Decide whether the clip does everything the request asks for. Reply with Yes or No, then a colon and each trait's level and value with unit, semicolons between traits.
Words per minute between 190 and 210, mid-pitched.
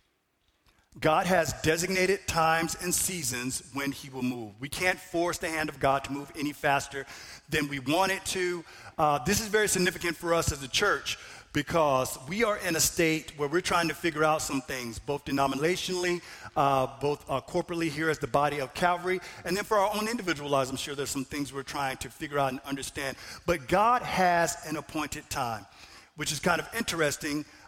Yes: average, 200 wpm; medium, 155 Hz